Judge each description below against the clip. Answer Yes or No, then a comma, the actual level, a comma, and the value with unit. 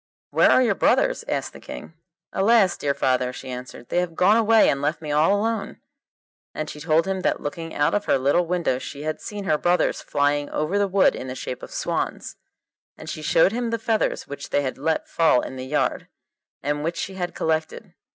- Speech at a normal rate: No, fast, 215 wpm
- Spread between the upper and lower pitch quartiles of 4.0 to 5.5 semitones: Yes, average, 5.1 semitones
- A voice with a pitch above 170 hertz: No, medium, 160 Hz